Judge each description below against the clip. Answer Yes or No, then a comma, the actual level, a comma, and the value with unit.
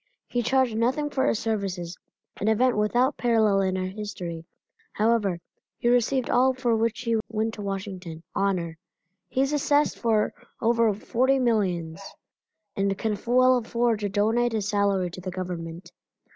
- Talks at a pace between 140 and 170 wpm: Yes, average, 155 wpm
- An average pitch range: Yes, average, 4.0 semitones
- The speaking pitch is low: No, high, 215 Hz